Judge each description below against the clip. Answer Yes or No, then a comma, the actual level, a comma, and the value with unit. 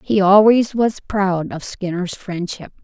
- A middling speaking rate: Yes, average, 150 wpm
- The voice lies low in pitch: No, high, 195 Hz